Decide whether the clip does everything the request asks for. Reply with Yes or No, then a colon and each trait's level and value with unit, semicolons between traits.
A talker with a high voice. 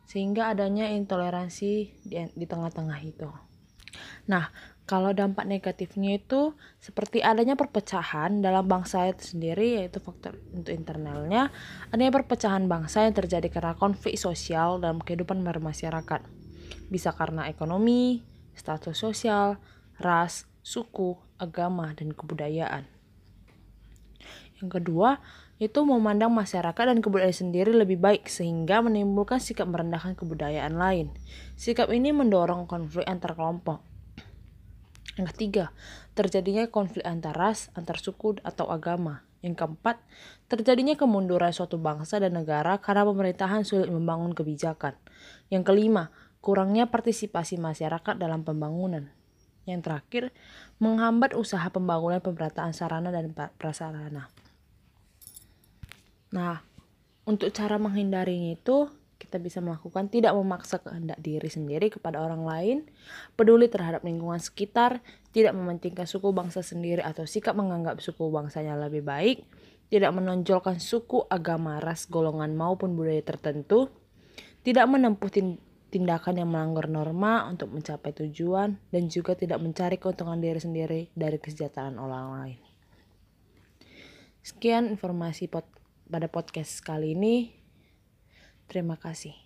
No: medium, 175 Hz